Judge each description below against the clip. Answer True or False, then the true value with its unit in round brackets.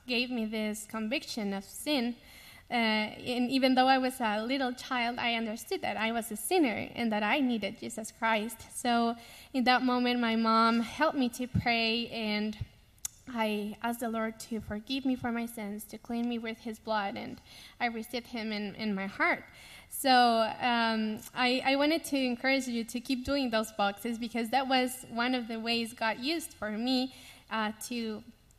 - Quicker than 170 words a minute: True (185 wpm)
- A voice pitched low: False (235 Hz)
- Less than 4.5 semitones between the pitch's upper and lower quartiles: True (2.4 semitones)